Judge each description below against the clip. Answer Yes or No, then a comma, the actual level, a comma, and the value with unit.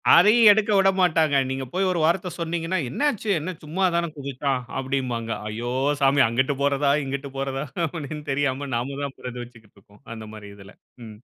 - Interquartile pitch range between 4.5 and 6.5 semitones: Yes, average, 5.0 semitones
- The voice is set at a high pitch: No, medium, 140 Hz